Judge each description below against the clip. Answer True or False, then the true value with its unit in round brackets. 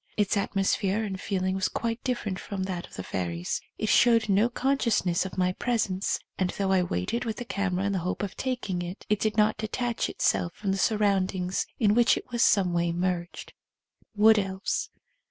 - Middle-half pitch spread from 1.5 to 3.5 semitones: True (3.0 semitones)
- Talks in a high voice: True (195 Hz)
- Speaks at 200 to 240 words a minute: True (205 wpm)